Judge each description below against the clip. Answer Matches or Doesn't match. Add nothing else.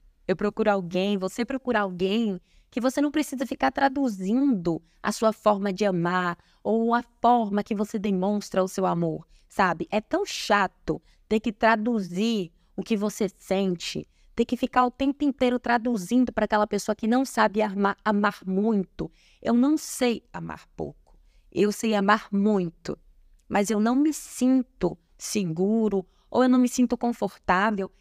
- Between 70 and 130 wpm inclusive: Doesn't match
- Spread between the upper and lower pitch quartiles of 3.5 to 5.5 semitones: Matches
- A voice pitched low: Doesn't match